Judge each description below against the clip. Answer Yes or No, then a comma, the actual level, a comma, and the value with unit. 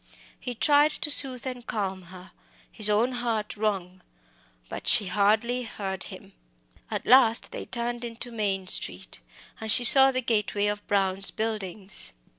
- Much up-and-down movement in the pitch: No, average, 3.6 semitones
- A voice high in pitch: Yes, high, 215 Hz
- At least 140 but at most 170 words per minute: Yes, average, 150 wpm